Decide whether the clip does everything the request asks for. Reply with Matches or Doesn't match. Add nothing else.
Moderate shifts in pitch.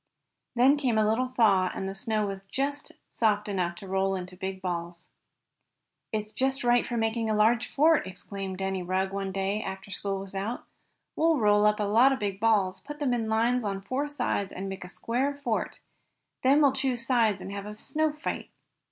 Matches